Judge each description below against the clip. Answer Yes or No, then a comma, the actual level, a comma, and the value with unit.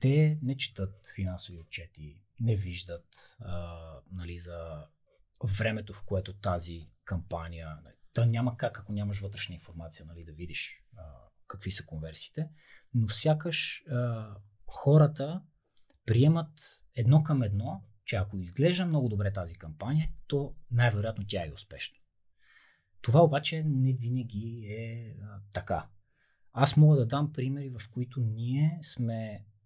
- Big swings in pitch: Yes, wide, 6.4 semitones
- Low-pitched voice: Yes, low, 110 Hz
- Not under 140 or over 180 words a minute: No, average, 130 wpm